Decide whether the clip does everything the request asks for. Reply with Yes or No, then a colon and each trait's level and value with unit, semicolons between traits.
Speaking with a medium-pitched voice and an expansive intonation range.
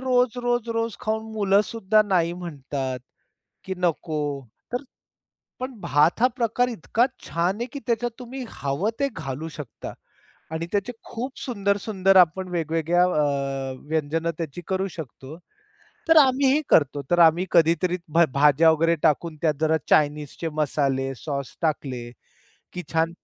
Yes: medium, 170 Hz; wide, 6.4 semitones